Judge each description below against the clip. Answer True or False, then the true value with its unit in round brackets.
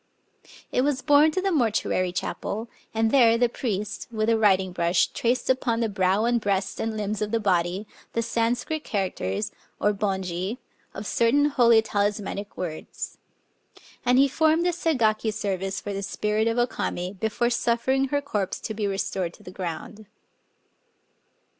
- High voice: True (220 Hz)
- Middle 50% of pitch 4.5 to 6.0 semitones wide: False (3.7 semitones)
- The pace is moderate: True (165 wpm)